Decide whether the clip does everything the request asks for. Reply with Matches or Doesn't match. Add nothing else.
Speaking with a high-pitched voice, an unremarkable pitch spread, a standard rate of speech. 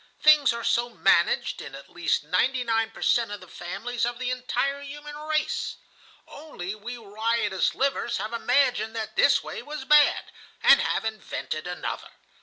Matches